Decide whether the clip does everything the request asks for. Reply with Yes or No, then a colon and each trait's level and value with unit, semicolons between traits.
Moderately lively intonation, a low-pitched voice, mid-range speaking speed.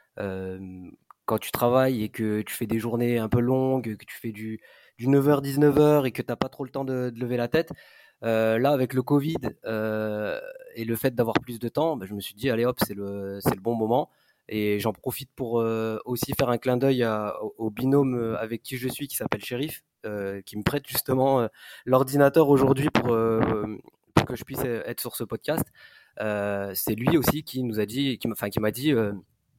No: average, 3.5 semitones; low, 120 Hz; fast, 230 wpm